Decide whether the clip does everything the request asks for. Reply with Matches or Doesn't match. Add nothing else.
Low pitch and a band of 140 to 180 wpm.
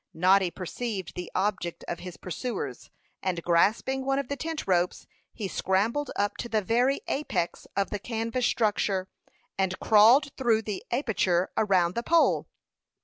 Doesn't match